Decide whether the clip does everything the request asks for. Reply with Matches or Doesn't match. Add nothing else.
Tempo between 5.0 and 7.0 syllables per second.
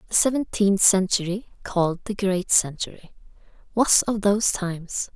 Doesn't match